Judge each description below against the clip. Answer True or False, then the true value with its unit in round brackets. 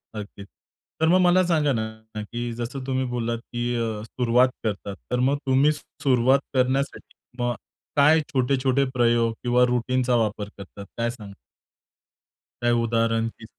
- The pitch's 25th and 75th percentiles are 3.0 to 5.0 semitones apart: False (2.5 semitones)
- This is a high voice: False (120 Hz)